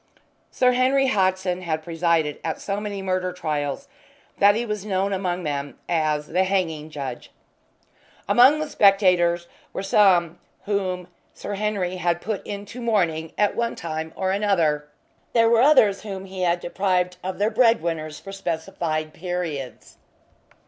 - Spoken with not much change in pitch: No, average, 3.7 semitones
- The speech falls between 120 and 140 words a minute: No, average, 150 wpm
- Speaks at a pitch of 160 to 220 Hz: Yes, medium, 185 Hz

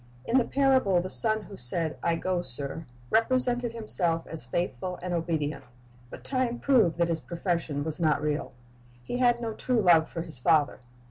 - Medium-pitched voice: Yes, medium, 175 Hz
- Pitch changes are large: Yes, wide, 6.4 semitones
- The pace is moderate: Yes, average, 180 wpm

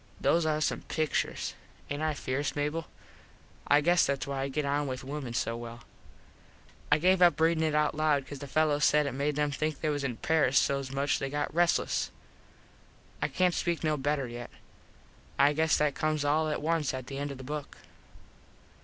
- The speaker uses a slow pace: No, average, 195 wpm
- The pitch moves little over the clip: Yes, narrow, 2.1 semitones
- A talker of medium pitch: Yes, medium, 145 Hz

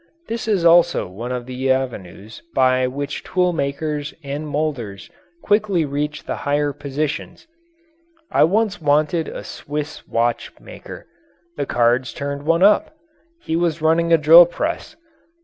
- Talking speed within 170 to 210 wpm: No, average, 140 wpm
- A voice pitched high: No, medium, 150 Hz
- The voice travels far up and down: No, average, 4.1 semitones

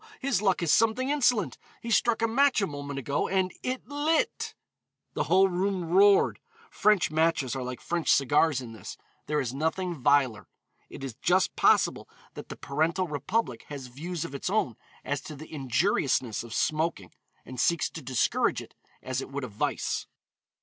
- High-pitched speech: No, medium, 160 Hz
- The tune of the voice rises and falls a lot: Yes, wide, 6.4 semitones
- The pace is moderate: Yes, average, 175 wpm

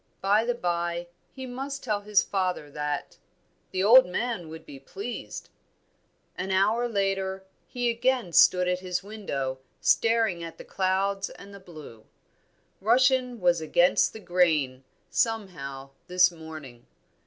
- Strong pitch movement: No, average, 4.7 semitones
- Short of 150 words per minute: Yes, slow, 135 wpm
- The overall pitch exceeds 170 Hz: Yes, high, 190 Hz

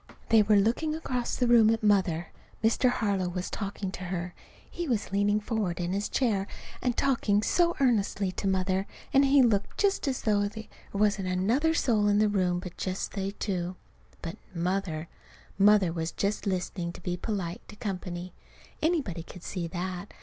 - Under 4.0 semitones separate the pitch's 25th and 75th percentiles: Yes, average, 3.6 semitones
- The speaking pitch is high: Yes, high, 200 Hz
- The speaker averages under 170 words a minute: No, average, 180 wpm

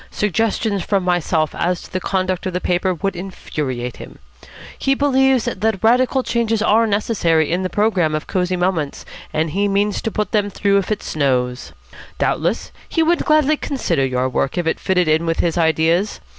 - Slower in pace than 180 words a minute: No, average, 185 wpm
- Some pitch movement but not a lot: Yes, average, 5.0 semitones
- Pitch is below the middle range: No, medium, 185 Hz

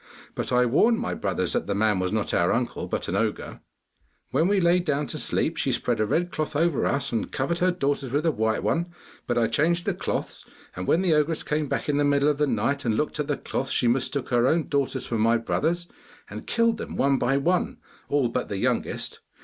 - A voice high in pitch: No, medium, 140 Hz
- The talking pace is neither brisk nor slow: No, fast, 235 wpm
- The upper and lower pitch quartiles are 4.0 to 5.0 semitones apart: No, wide, 5.4 semitones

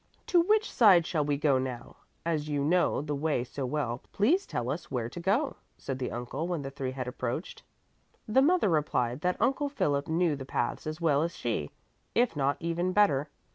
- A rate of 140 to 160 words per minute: No, average, 200 wpm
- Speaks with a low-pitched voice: No, medium, 150 Hz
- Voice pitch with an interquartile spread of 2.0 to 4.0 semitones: No, average, 5.3 semitones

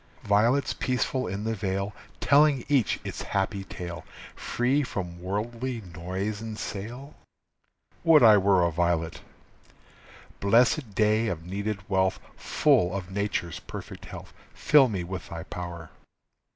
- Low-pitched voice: Yes, low, 100 Hz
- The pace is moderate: No, slow, 130 wpm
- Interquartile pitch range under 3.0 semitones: No, average, 4.5 semitones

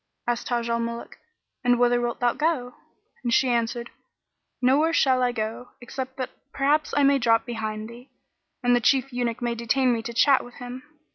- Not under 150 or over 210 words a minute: Yes, average, 190 wpm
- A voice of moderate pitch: No, high, 245 Hz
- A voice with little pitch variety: Yes, narrow, 1.8 semitones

